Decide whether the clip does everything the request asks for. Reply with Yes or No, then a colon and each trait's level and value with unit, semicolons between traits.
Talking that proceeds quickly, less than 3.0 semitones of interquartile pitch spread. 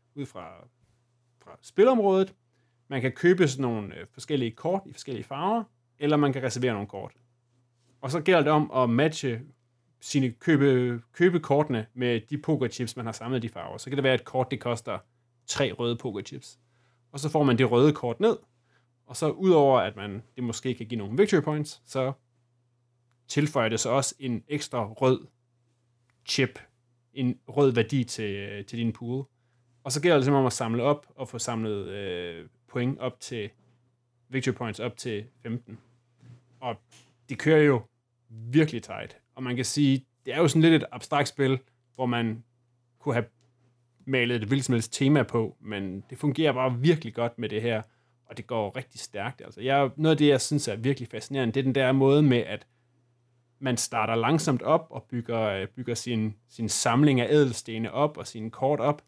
No: average, 185 wpm; narrow, 2.5 semitones